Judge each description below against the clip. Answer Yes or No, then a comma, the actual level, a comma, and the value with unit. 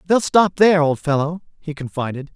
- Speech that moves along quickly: No, average, 180 wpm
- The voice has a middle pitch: Yes, medium, 160 Hz